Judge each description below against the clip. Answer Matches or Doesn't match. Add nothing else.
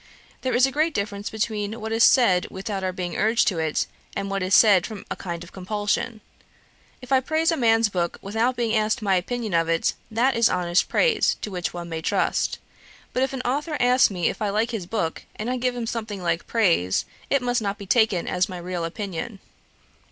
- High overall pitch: Matches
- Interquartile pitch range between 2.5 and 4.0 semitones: Doesn't match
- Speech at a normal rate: Doesn't match